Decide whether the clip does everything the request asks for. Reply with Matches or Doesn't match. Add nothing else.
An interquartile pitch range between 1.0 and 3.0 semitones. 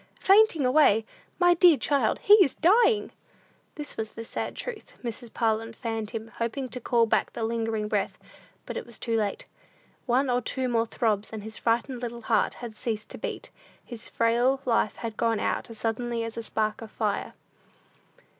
Matches